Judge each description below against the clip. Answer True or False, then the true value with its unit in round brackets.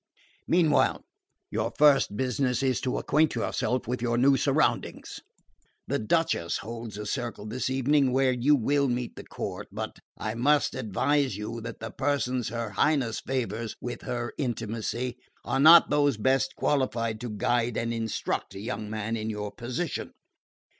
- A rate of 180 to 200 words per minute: False (155 wpm)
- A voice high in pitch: False (120 Hz)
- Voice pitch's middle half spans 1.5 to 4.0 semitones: True (3.2 semitones)